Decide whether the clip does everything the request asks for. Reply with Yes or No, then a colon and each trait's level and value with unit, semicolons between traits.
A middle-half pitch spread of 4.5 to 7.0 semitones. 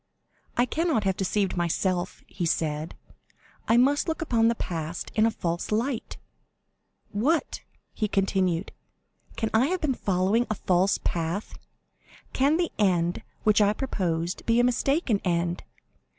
Yes: wide, 5.5 semitones